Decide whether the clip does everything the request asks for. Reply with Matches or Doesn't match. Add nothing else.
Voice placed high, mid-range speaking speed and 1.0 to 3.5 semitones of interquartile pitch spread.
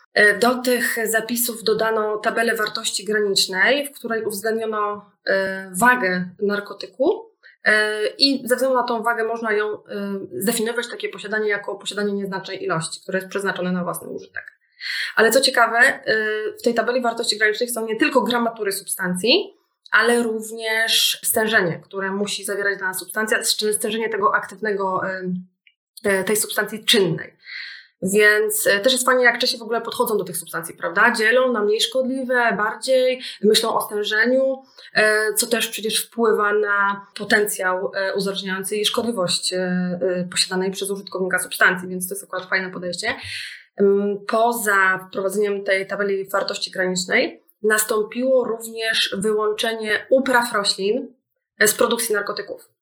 Matches